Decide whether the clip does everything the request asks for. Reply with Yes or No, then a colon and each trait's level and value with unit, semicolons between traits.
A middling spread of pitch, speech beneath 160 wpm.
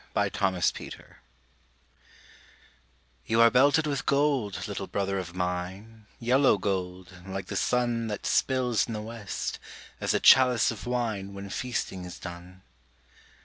Yes: average, 4.6 semitones; average, 140 wpm